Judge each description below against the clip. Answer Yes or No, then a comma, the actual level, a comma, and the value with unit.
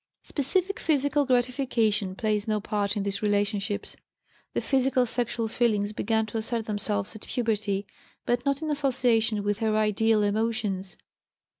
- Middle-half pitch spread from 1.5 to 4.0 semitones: Yes, average, 3.1 semitones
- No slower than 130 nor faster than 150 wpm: Yes, average, 140 wpm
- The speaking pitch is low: No, high, 220 Hz